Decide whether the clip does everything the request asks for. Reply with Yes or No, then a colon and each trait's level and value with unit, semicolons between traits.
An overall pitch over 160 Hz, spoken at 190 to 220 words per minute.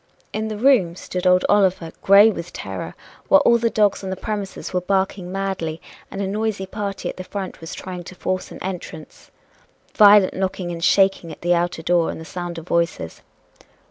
Yes: high, 190 Hz; average, 195 wpm